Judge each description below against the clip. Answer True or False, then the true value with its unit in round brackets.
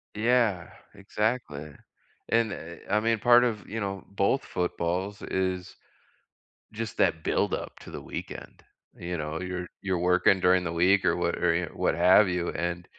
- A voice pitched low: True (95 Hz)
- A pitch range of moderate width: True (3.3 semitones)